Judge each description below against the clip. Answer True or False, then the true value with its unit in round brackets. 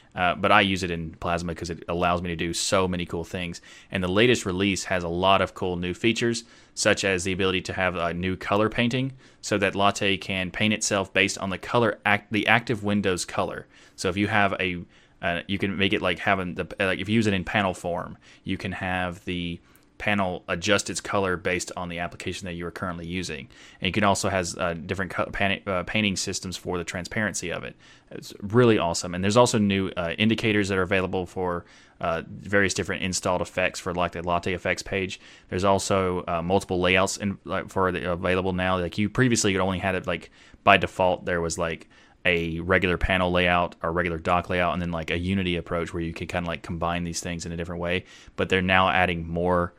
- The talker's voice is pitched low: True (95 Hz)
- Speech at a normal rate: False (230 wpm)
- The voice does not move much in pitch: True (2.2 semitones)